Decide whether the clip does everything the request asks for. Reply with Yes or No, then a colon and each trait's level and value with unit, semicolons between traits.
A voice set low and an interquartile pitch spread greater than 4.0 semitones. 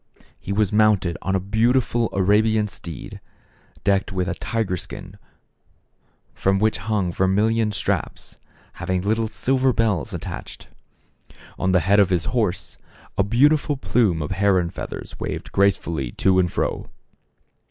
No: low, 100 Hz; average, 3.1 semitones